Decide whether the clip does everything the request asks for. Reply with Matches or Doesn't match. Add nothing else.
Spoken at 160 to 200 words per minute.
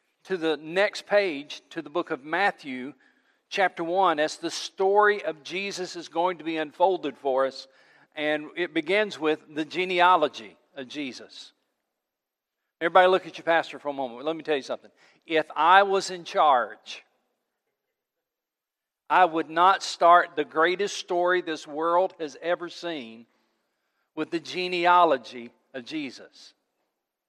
Doesn't match